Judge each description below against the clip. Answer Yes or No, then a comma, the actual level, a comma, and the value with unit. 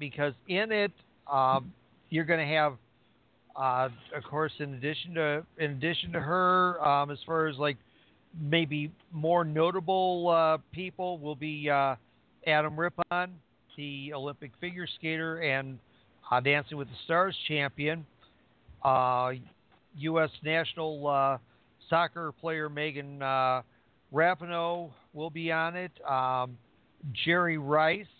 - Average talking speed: No, slow, 130 wpm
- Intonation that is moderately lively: Yes, average, 3.6 semitones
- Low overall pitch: No, medium, 150 Hz